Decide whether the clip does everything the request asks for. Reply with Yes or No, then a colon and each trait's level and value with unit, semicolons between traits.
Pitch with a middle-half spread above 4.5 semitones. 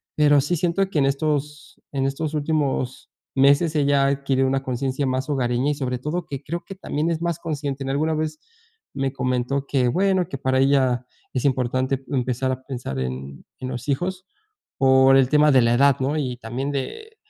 No: narrow, 2.5 semitones